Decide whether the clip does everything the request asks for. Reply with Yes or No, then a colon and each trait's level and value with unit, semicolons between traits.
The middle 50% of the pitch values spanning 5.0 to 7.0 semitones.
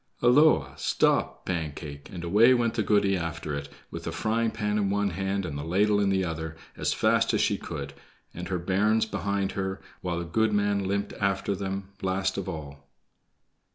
No: average, 3.3 semitones